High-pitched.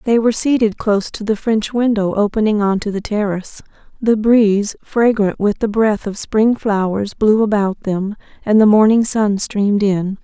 Yes: high, 210 Hz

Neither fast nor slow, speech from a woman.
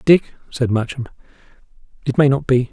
No: average, 155 wpm; male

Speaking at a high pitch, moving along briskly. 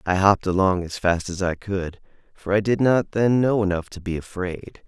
No: very low, 95 Hz; fast, 220 wpm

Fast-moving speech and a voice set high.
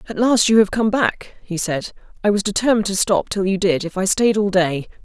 Yes: fast, 250 wpm; high, 200 Hz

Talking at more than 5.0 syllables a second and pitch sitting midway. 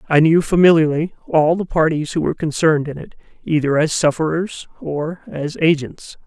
Yes: 5.2 syllables/s; medium, 155 Hz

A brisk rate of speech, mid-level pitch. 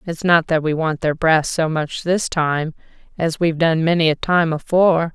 Yes: fast, 210 wpm; medium, 165 Hz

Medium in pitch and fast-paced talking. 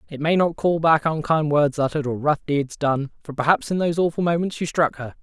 Yes: medium, 155 Hz; fast, 230 wpm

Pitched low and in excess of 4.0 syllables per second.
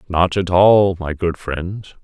No: very low, 90 Hz; 3.4 syllables/s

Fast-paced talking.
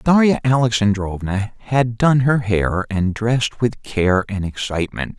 No: average, 140 wpm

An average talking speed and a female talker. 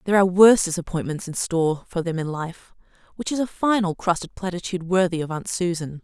No: fast, 210 wpm; female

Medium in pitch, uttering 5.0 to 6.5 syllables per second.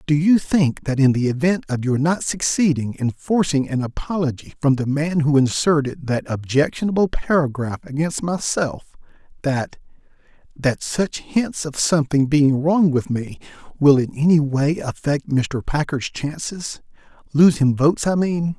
No: medium, 150 Hz; 4.5 syllables/s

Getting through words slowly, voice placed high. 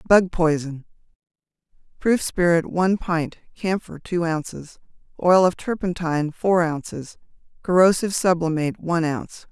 No: slow, 105 wpm; medium, 170 Hz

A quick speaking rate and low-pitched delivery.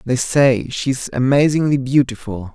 No: average, 140 wpm; low, 130 Hz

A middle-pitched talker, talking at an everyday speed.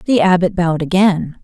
Yes: medium, 180 Hz; average, 170 wpm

